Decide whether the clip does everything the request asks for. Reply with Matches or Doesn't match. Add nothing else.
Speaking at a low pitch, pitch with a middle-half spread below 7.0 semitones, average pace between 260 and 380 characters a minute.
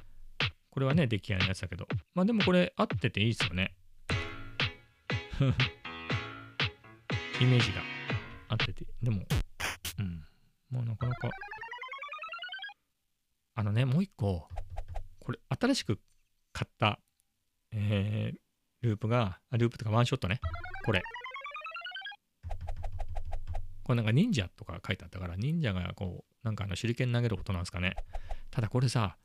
Matches